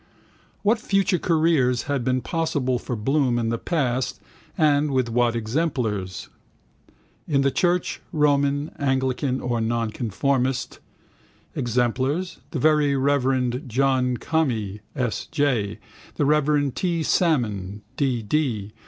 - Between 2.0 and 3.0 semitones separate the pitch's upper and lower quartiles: No, average, 3.8 semitones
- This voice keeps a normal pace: No, slow, 115 wpm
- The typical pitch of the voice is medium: No, low, 130 Hz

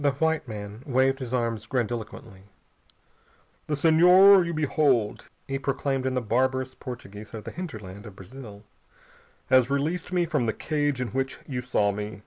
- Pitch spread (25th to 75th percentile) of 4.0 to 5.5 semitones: Yes, average, 4.8 semitones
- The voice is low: Yes, low, 130 Hz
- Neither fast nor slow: Yes, average, 160 wpm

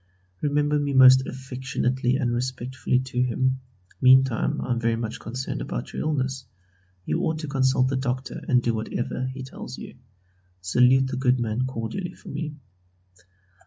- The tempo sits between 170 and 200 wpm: No, average, 160 wpm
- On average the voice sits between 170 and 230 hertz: No, low, 130 Hz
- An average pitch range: No, narrow, 1.3 semitones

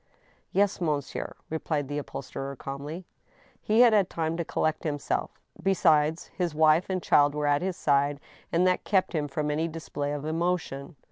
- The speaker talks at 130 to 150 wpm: No, average, 175 wpm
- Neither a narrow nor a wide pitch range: Yes, average, 3.4 semitones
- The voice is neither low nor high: Yes, medium, 155 Hz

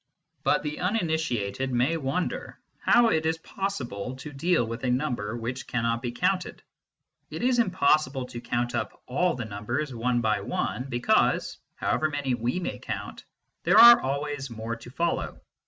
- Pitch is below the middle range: Yes, low, 130 Hz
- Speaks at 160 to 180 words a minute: Yes, average, 165 wpm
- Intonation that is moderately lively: Yes, average, 5.0 semitones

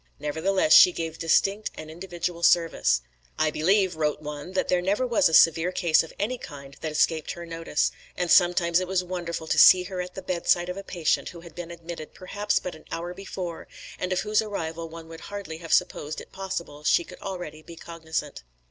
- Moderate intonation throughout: No, narrow, 2.3 semitones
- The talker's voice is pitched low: No, medium, 170 Hz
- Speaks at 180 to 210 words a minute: Yes, fast, 205 wpm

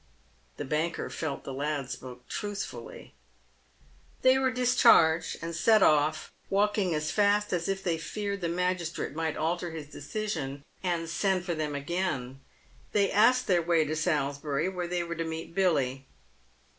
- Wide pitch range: No, average, 4.3 semitones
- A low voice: No, medium, 170 Hz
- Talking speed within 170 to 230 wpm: No, average, 155 wpm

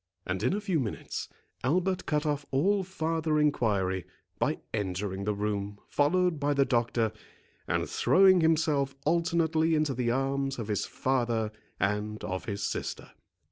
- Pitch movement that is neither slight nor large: No, wide, 7.2 semitones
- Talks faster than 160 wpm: No, average, 145 wpm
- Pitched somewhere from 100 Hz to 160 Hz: Yes, low, 135 Hz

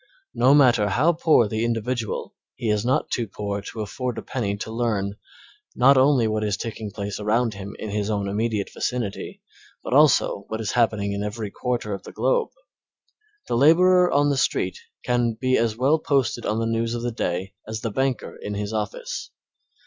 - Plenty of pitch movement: No, average, 3.4 semitones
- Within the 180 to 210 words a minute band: Yes, average, 190 wpm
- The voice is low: Yes, low, 115 Hz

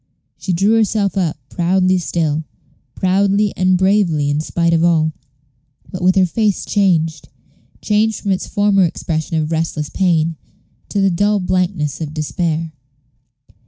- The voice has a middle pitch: Yes, medium, 180 Hz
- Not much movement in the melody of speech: No, average, 3.4 semitones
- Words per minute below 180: Yes, average, 140 wpm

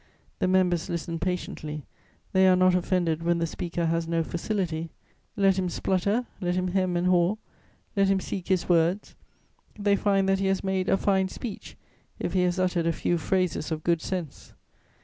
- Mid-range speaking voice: Yes, medium, 180 Hz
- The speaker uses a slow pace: No, average, 185 wpm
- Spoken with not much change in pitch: Yes, narrow, 2.1 semitones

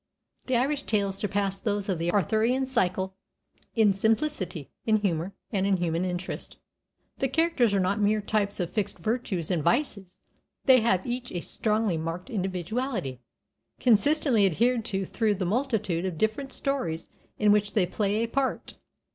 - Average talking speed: Yes, average, 160 wpm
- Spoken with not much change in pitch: No, average, 4.2 semitones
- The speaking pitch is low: No, high, 205 Hz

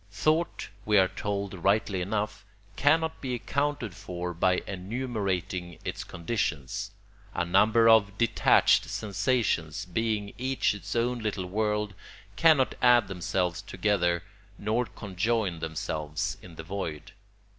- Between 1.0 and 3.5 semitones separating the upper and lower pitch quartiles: No, average, 4.2 semitones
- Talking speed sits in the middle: No, slow, 120 wpm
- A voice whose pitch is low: Yes, low, 100 Hz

